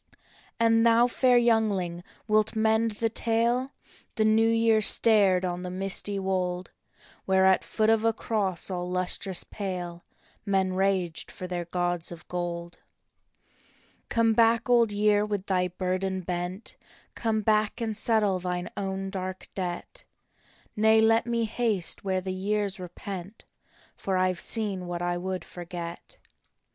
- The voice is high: Yes, high, 195 Hz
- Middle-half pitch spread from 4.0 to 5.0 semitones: No, average, 3.4 semitones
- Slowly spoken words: No, average, 150 wpm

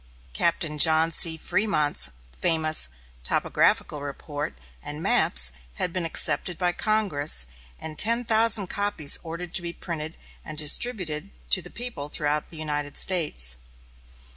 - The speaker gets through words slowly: Yes, slow, 130 wpm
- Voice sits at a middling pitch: Yes, medium, 160 Hz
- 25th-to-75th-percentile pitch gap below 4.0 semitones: Yes, average, 3.5 semitones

